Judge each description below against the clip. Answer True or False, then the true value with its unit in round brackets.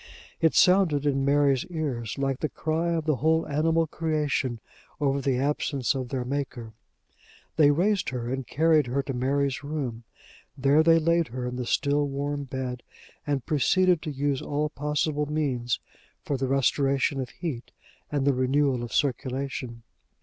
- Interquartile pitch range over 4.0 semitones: False (2.7 semitones)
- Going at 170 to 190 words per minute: False (160 wpm)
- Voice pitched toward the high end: False (140 Hz)